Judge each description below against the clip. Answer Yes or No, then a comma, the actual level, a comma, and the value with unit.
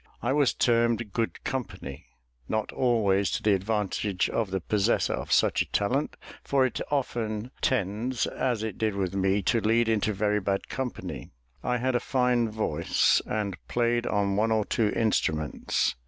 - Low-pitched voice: Yes, low, 110 Hz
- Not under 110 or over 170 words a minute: Yes, average, 165 wpm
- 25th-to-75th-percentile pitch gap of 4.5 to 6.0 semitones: No, average, 3.2 semitones